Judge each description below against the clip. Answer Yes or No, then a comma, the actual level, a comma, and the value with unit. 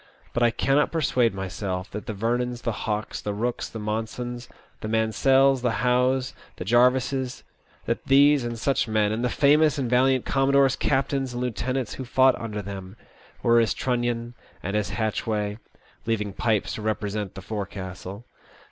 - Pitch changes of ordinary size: Yes, average, 3.5 semitones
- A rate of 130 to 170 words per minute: Yes, average, 160 wpm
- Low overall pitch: Yes, low, 120 Hz